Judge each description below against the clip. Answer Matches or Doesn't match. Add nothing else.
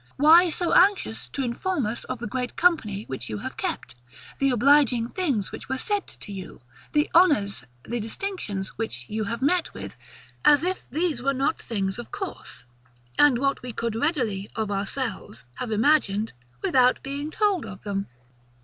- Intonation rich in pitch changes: Matches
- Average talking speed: Matches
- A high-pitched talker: Matches